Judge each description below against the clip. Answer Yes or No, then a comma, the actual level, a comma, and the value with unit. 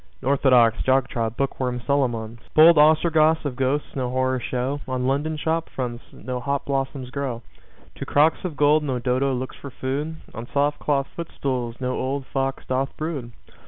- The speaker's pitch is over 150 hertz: No, low, 135 Hz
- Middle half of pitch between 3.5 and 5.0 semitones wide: No, narrow, 2.5 semitones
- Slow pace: No, average, 170 wpm